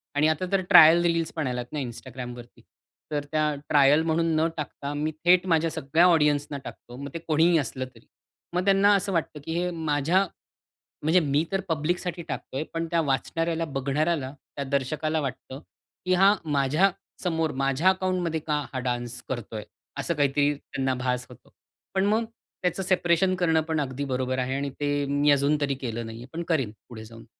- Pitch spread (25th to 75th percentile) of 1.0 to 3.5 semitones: No, average, 3.9 semitones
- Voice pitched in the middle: Yes, medium, 150 Hz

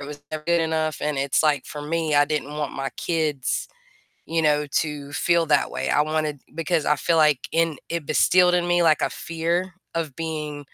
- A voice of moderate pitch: Yes, medium, 155 Hz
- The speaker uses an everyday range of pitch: No, narrow, 2.0 semitones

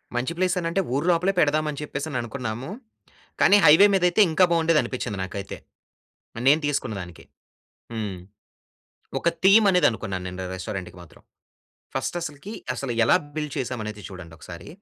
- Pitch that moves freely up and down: Yes, wide, 8.0 semitones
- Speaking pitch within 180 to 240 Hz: No, medium, 140 Hz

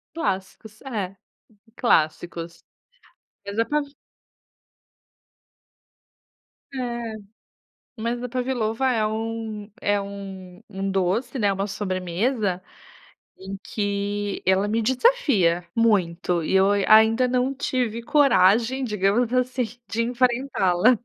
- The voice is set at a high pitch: Yes, high, 215 Hz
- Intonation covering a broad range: No, average, 4.2 semitones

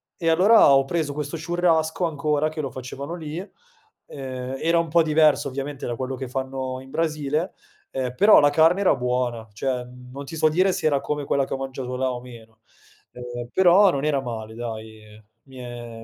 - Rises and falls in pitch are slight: No, average, 4.1 semitones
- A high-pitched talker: No, low, 135 Hz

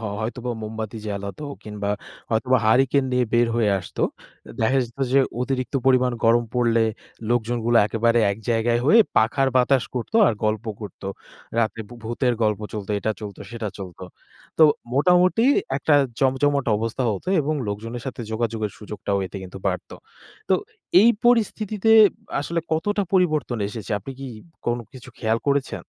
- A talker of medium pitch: No, low, 120 Hz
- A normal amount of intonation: Yes, average, 3.6 semitones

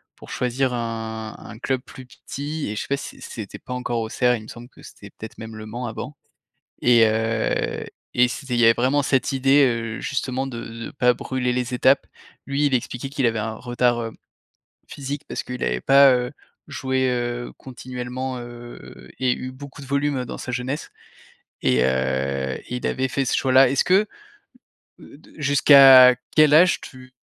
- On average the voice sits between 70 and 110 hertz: No, low, 125 Hz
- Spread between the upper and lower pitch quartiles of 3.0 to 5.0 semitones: No, narrow, 2.5 semitones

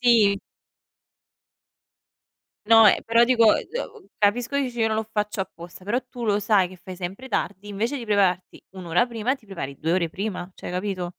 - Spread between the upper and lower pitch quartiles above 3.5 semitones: Yes, average, 4.0 semitones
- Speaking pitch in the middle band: No, high, 210 Hz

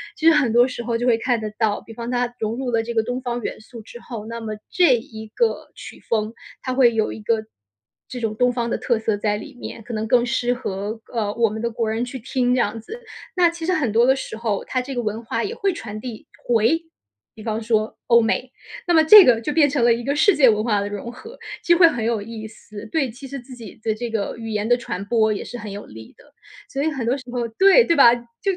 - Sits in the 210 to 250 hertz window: Yes, high, 235 Hz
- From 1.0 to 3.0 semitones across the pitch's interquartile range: Yes, average, 2.7 semitones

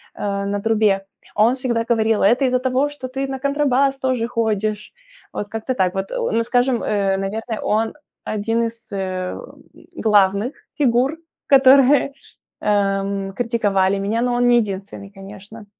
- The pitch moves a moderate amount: Yes, average, 4.0 semitones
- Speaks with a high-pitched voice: Yes, high, 225 Hz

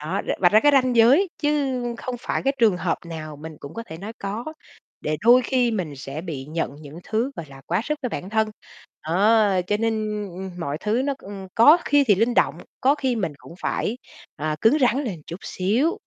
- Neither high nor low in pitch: No, high, 210 Hz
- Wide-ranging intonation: Yes, wide, 6.9 semitones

